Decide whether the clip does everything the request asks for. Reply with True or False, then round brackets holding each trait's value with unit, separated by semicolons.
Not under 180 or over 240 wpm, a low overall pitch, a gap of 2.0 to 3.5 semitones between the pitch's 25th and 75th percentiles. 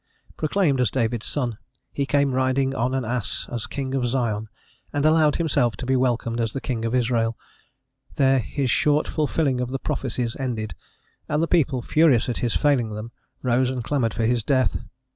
True (185 wpm; 130 Hz; 2.9 semitones)